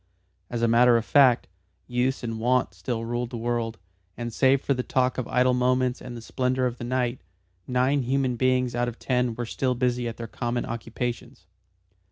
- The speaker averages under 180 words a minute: No, average, 195 wpm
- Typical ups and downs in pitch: No, narrow, 1.4 semitones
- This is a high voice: No, low, 125 Hz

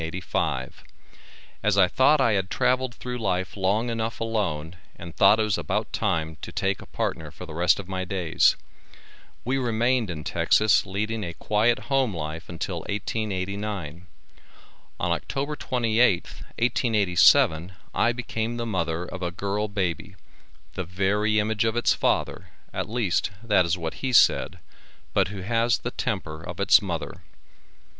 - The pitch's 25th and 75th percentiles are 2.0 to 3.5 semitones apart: No, average, 4.3 semitones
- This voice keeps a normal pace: Yes, average, 150 wpm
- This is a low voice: Yes, low, 100 Hz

